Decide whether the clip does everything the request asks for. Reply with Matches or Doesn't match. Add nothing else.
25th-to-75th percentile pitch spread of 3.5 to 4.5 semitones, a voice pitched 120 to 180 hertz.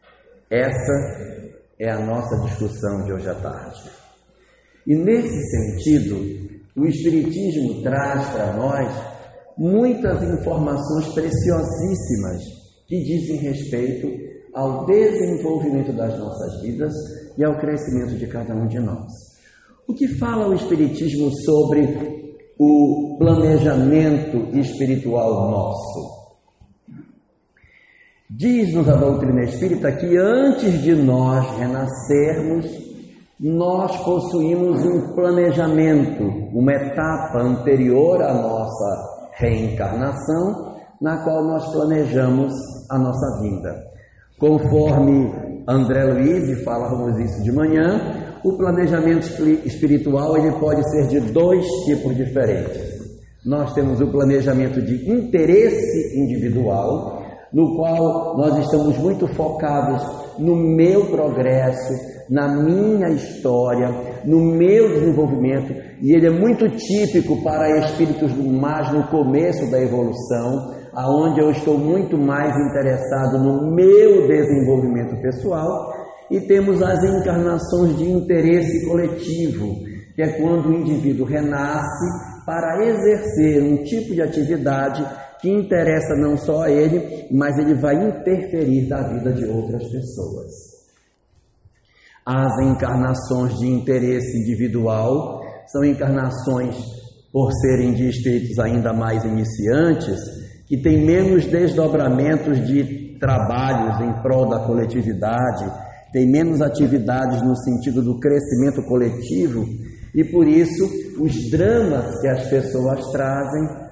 Matches